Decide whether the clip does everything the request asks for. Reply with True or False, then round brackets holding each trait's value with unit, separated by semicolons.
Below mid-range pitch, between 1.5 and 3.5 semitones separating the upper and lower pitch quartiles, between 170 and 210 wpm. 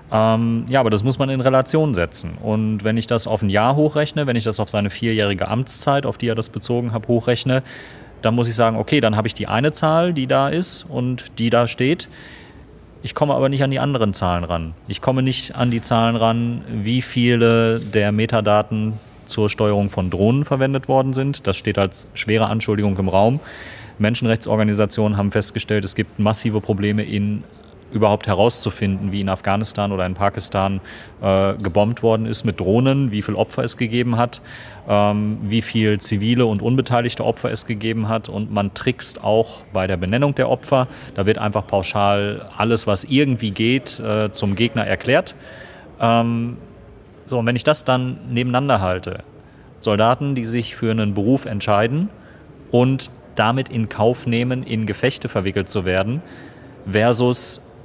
True (115 Hz; 3.0 semitones; 175 wpm)